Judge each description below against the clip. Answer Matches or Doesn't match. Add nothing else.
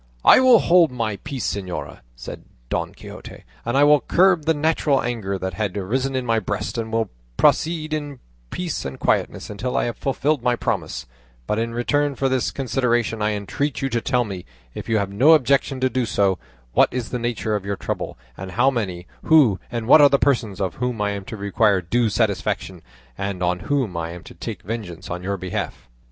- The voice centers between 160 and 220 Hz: Doesn't match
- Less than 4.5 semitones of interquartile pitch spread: Doesn't match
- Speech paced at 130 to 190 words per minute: Doesn't match